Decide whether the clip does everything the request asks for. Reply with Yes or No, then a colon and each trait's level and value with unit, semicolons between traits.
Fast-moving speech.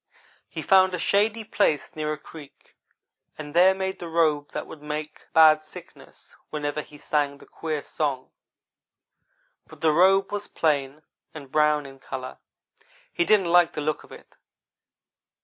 No: average, 155 wpm